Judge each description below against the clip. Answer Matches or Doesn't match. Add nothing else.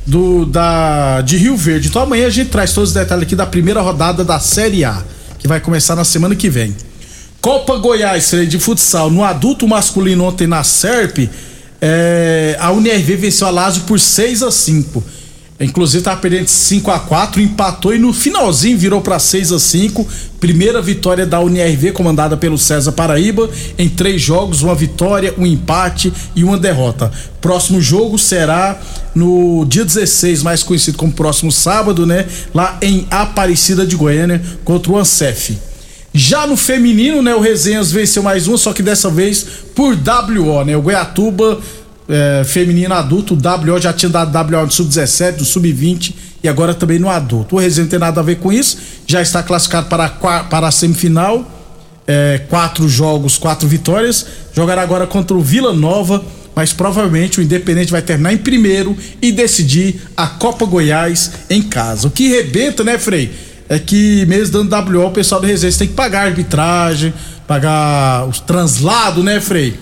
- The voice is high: Doesn't match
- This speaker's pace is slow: Doesn't match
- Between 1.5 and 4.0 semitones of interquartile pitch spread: Matches